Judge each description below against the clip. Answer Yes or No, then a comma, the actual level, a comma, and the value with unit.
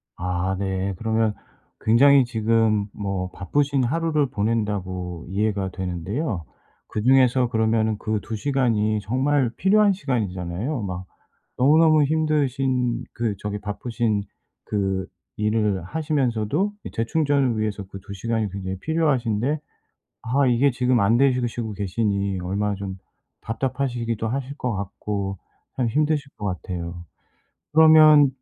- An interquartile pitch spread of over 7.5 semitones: No, average, 5.2 semitones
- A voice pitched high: No, low, 115 Hz